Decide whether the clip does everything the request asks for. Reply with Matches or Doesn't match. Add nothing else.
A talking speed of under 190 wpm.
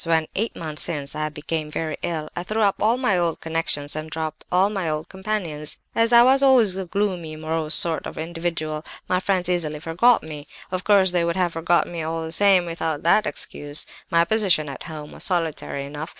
Doesn't match